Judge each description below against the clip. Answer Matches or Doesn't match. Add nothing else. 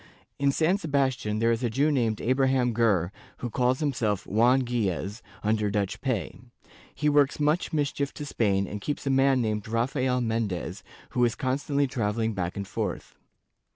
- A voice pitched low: Matches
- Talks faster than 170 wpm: Doesn't match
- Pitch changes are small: Doesn't match